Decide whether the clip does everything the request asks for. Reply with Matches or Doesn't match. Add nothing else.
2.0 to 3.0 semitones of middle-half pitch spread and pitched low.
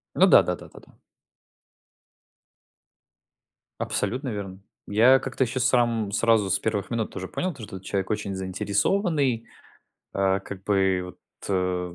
Doesn't match